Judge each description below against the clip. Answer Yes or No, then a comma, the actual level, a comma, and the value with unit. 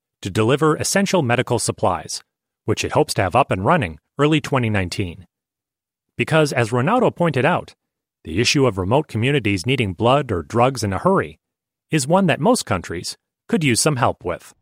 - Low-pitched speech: Yes, low, 125 Hz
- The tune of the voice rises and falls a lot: Yes, wide, 5.8 semitones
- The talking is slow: No, average, 170 wpm